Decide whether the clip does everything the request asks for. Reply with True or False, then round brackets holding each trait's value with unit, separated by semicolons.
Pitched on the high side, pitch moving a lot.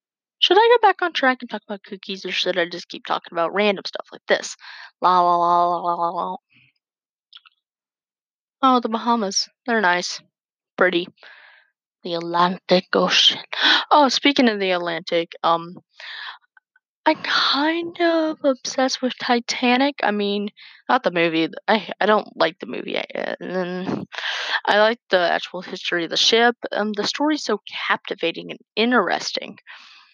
True (210 Hz; 6.5 semitones)